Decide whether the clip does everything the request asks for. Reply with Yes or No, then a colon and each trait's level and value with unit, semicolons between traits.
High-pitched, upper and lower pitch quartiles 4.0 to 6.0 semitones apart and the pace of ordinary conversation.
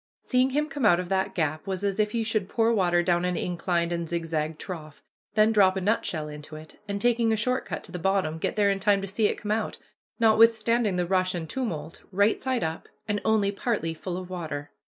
No: high, 195 Hz; average, 4.3 semitones; fast, 230 wpm